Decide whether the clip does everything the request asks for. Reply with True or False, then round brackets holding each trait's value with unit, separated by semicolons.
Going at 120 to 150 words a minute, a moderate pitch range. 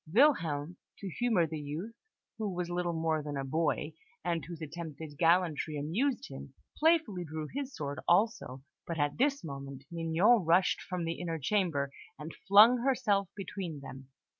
False (160 wpm; 5.0 semitones)